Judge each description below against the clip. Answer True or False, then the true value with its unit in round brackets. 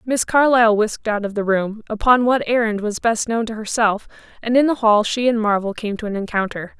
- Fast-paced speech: True (230 wpm)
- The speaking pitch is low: False (220 Hz)